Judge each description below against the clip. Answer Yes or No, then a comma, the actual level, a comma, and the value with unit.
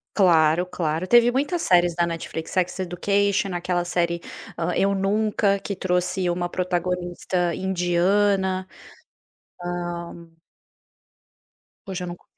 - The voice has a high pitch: No, medium, 180 Hz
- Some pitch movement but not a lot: No, narrow, 2.0 semitones